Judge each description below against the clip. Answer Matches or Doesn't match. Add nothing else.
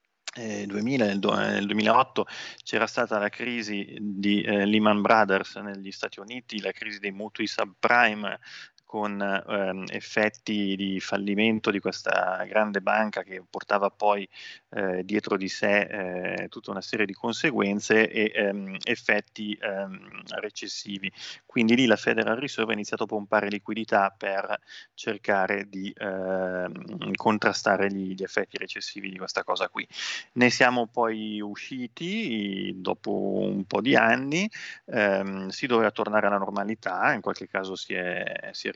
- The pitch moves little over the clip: Matches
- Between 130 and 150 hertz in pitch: Doesn't match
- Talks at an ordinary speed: Matches